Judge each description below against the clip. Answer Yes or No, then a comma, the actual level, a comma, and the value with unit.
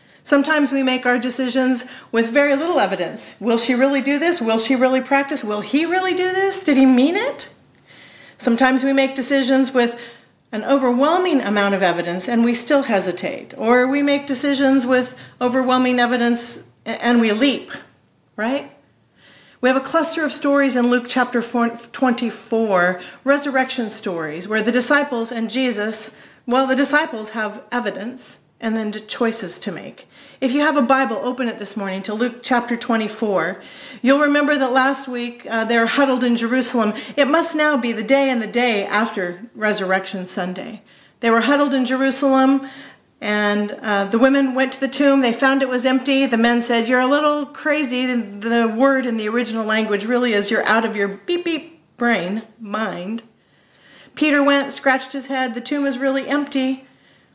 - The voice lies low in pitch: No, very high, 250 Hz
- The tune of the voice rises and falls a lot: No, average, 3.4 semitones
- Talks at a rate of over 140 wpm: Yes, average, 175 wpm